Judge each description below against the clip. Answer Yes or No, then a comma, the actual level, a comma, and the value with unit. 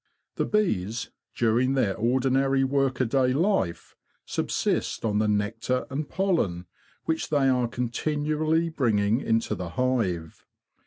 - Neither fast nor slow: No, slow, 120 wpm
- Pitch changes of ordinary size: Yes, average, 4.3 semitones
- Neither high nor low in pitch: No, low, 125 Hz